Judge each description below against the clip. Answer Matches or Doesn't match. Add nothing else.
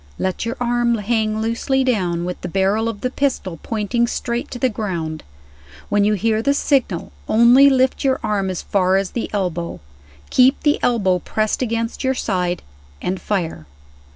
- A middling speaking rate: Matches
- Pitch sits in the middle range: Doesn't match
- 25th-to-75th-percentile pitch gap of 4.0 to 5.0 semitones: Matches